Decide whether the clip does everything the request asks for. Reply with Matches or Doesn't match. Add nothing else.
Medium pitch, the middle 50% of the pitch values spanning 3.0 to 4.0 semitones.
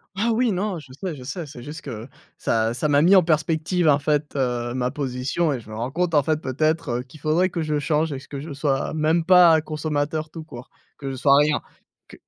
Matches